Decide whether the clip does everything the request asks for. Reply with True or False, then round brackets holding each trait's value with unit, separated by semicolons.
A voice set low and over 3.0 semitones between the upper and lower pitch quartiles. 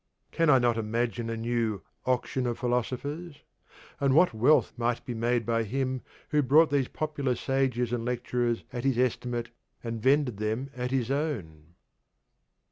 False (125 Hz; 2.7 semitones)